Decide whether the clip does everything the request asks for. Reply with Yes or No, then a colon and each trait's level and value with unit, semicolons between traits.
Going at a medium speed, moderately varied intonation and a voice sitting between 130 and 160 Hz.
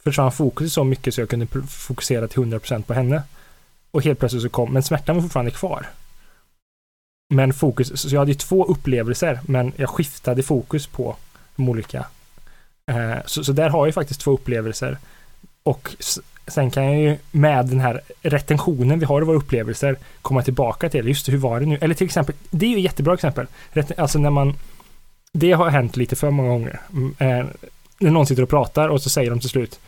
No: fast, 200 wpm; average, 3.2 semitones; medium, 140 Hz